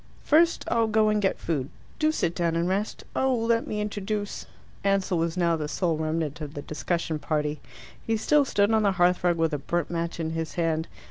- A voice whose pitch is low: No, medium, 175 Hz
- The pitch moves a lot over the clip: No, average, 4.5 semitones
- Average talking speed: No, fast, 210 wpm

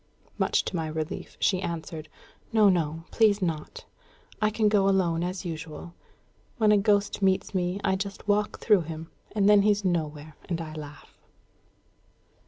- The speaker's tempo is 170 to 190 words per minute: No, average, 160 wpm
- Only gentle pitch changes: No, average, 4.0 semitones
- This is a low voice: No, medium, 185 Hz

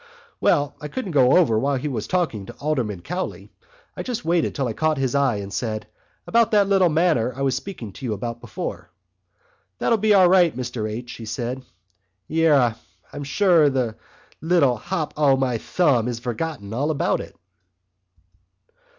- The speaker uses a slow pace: No, average, 170 wpm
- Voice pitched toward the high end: No, low, 135 Hz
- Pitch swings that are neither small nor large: No, wide, 5.9 semitones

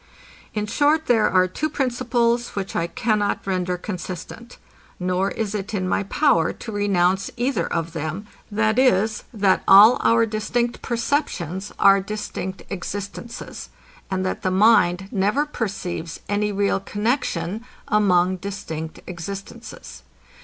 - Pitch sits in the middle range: No, high, 205 Hz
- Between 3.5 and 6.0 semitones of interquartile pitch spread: Yes, average, 3.8 semitones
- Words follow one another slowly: Yes, slow, 125 wpm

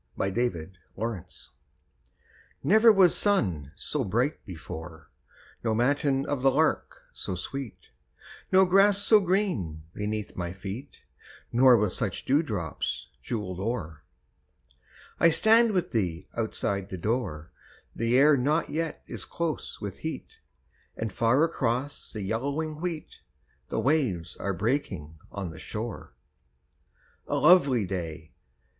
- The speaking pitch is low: Yes, low, 120 Hz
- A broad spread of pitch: Yes, wide, 8.3 semitones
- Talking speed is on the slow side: Yes, slow, 125 wpm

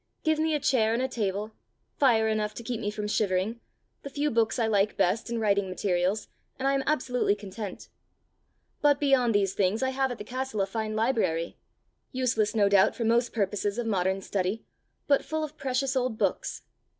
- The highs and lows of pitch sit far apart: No, average, 4.3 semitones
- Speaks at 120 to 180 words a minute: No, average, 195 wpm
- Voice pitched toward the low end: No, high, 220 Hz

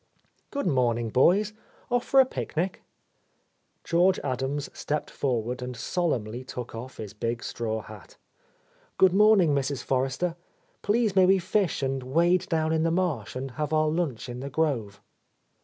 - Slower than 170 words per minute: Yes, average, 155 wpm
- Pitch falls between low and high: Yes, medium, 145 Hz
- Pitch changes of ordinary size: No, wide, 6.1 semitones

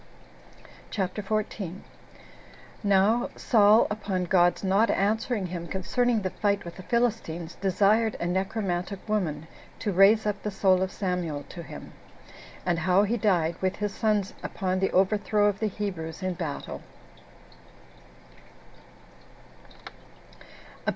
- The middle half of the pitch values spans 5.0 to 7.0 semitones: No, average, 2.7 semitones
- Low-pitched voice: No, high, 195 Hz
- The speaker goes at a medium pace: No, slow, 125 wpm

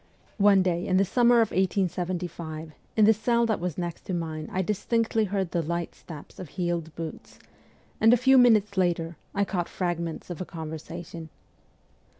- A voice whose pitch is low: No, medium, 180 Hz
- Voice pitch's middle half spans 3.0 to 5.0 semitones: Yes, average, 3.5 semitones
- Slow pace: No, average, 170 wpm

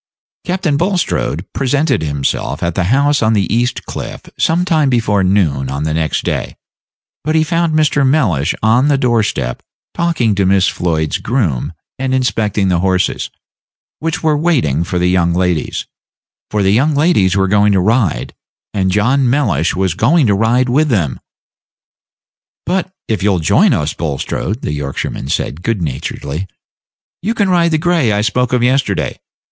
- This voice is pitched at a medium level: No, low, 110 Hz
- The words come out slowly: No, average, 165 wpm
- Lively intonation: Yes, wide, 8.1 semitones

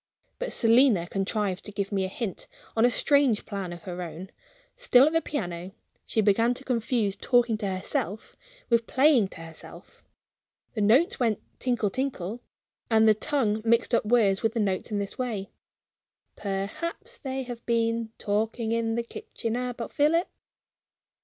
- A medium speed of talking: Yes, average, 160 wpm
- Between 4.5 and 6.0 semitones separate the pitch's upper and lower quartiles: No, average, 3.7 semitones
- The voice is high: Yes, high, 225 Hz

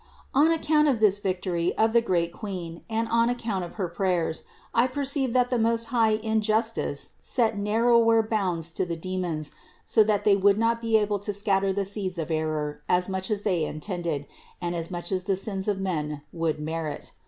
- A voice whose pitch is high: Yes, high, 200 Hz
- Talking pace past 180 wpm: Yes, average, 200 wpm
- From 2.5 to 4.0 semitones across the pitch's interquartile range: No, average, 4.6 semitones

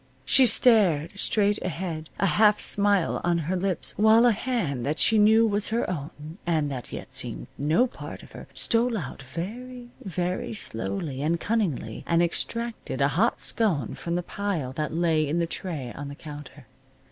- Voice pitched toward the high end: No, medium, 175 Hz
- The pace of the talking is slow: No, average, 175 wpm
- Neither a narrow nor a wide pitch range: No, wide, 6.3 semitones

